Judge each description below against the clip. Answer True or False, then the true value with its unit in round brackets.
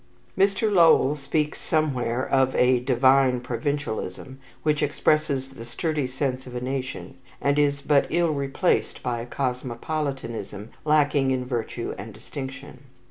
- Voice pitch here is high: False (135 Hz)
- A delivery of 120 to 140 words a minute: True (135 wpm)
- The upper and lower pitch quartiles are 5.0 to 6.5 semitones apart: False (2.9 semitones)